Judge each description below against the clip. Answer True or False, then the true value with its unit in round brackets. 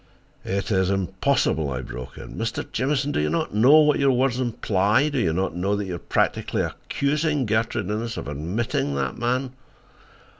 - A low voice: True (110 Hz)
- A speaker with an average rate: True (165 wpm)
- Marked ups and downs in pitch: True (6.2 semitones)